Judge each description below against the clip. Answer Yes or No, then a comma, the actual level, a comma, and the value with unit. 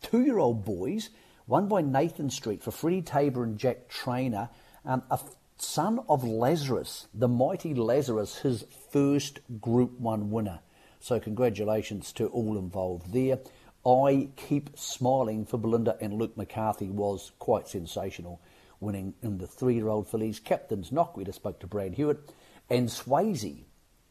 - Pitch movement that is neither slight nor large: Yes, average, 4.3 semitones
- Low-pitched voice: Yes, low, 115 Hz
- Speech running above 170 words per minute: No, average, 155 wpm